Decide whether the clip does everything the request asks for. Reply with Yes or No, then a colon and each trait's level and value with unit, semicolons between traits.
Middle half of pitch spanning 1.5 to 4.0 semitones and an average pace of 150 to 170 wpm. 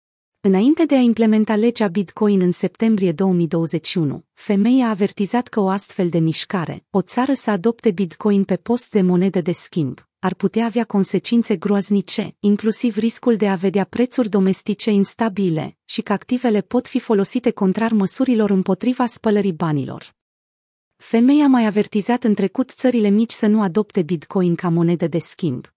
Yes: average, 3.4 semitones; average, 155 wpm